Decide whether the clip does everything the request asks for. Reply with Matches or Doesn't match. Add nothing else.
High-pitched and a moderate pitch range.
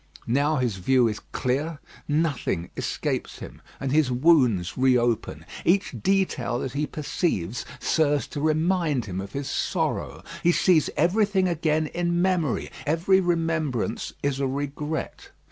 Doesn't match